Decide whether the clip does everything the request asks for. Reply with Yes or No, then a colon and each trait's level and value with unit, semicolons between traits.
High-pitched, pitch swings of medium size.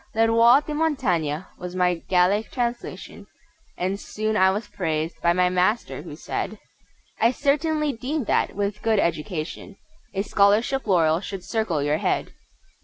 Yes: high, 200 Hz; average, 4.7 semitones